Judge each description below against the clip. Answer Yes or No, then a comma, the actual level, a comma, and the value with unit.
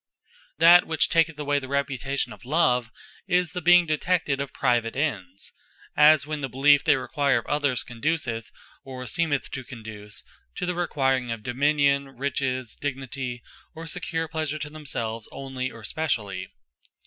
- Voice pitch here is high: No, medium, 140 Hz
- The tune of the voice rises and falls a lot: No, average, 3.7 semitones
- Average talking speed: Yes, average, 150 wpm